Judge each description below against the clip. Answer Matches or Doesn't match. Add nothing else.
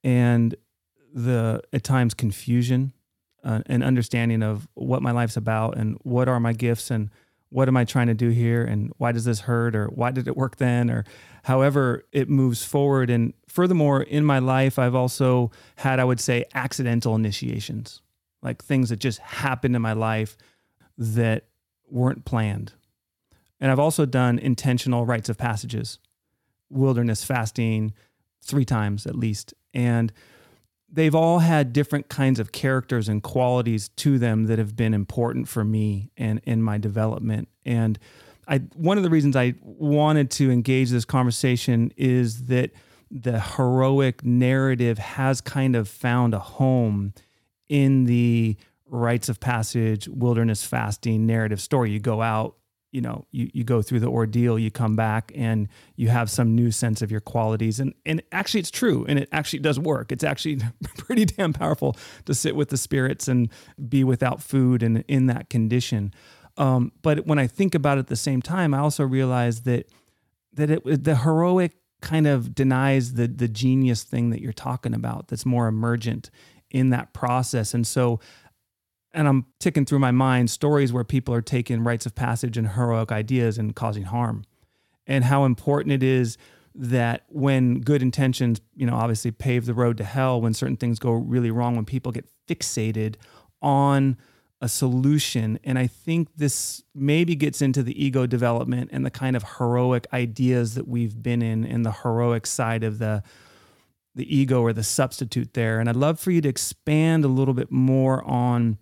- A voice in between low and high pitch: Doesn't match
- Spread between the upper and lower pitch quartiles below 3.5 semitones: Matches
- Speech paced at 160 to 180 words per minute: Matches